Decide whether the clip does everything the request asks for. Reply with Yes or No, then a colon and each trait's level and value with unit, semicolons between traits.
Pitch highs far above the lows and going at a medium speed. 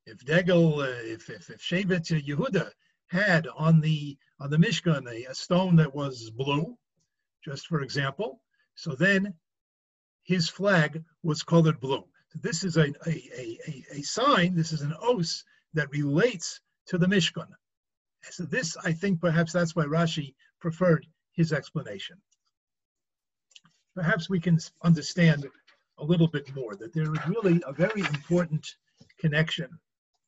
No: average, 2.8 semitones; average, 145 wpm